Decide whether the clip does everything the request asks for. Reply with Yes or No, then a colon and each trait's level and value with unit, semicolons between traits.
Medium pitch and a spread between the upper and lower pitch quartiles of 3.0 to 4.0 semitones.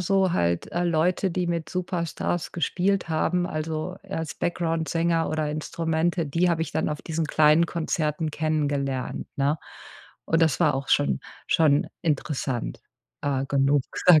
No: medium, 160 Hz; narrow, 2.5 semitones